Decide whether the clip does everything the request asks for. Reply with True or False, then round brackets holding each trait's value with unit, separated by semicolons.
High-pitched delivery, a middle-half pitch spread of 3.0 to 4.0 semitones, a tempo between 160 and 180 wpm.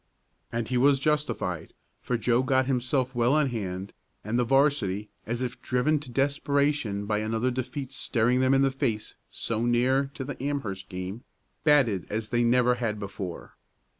False (125 Hz; 3.7 semitones; 165 wpm)